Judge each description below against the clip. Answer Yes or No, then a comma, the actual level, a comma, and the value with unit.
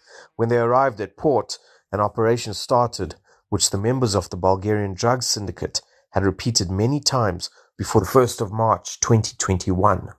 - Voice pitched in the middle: No, low, 105 Hz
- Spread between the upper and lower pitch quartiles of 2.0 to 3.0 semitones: No, average, 3.6 semitones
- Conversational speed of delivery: Yes, average, 155 wpm